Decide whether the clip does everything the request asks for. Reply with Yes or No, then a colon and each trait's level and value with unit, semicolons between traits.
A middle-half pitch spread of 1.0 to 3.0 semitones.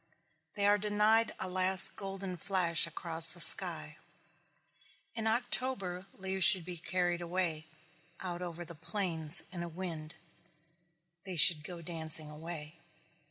Yes: narrow, 2.6 semitones